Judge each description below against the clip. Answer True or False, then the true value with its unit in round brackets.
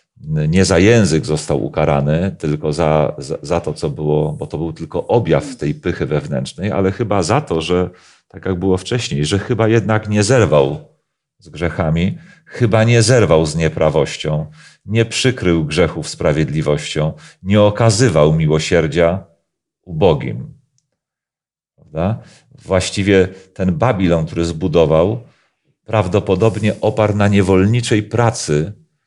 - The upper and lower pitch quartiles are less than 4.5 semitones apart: False (5.5 semitones)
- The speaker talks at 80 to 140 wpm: True (125 wpm)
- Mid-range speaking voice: False (95 Hz)